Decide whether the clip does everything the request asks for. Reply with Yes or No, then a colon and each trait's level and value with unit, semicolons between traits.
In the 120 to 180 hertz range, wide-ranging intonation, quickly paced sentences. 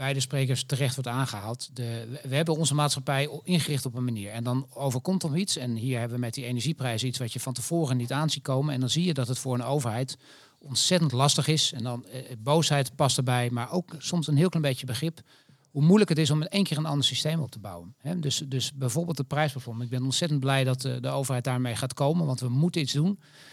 No: low, 135 Hz; average, 3.3 semitones; fast, 245 wpm